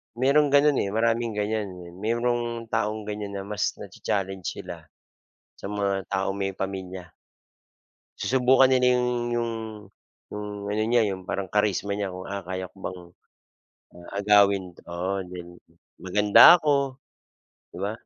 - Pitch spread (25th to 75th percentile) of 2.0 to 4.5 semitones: Yes, average, 3.4 semitones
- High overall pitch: No, low, 105 Hz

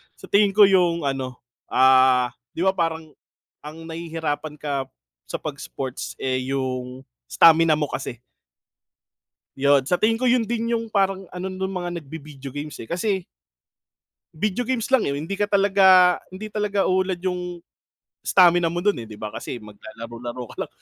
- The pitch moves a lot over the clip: Yes, wide, 6.1 semitones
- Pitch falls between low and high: Yes, medium, 170 Hz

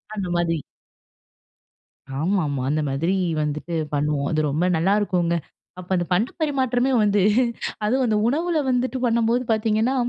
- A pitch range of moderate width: No, wide, 6.6 semitones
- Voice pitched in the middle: No, high, 200 Hz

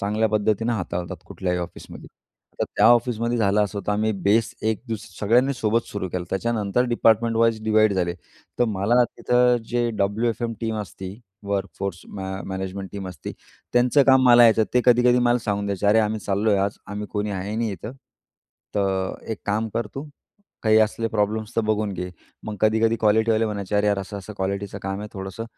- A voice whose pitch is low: Yes, low, 105 Hz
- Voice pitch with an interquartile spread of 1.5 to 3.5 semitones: Yes, narrow, 2.5 semitones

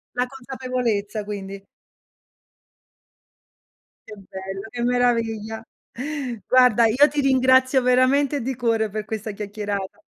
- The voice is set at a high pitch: Yes, high, 230 Hz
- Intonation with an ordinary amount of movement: Yes, average, 3.5 semitones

